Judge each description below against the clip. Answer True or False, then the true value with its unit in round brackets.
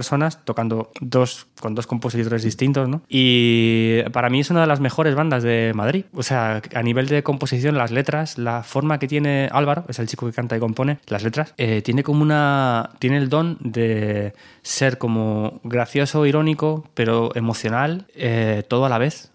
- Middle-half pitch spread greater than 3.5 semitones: True (3.9 semitones)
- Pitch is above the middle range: False (130 Hz)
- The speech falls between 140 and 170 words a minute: False (185 wpm)